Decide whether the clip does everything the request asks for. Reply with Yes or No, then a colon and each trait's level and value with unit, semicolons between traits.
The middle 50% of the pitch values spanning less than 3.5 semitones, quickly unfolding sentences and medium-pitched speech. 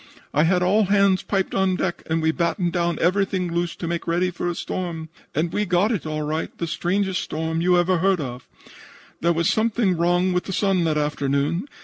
Yes: narrow, 2.5 semitones; fast, 215 wpm; medium, 175 Hz